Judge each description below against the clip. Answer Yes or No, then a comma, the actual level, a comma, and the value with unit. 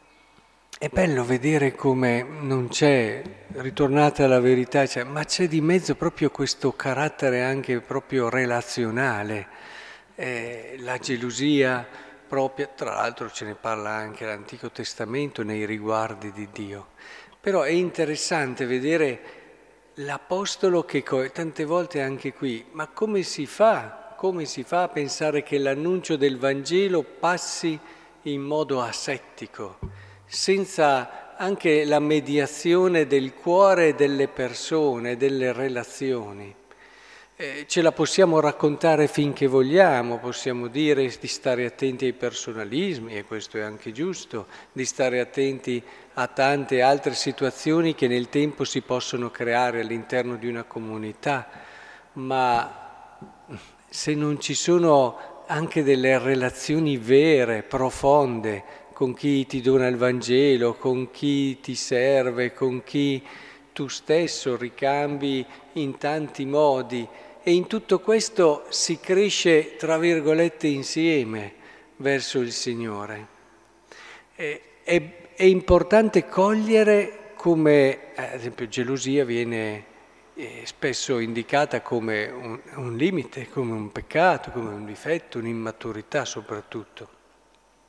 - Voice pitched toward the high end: No, low, 135 Hz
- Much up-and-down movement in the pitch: No, average, 4.2 semitones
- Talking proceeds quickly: No, slow, 115 wpm